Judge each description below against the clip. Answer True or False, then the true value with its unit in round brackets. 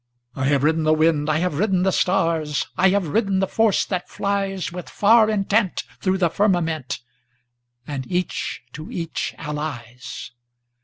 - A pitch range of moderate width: True (4.0 semitones)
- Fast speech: False (135 wpm)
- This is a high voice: False (175 Hz)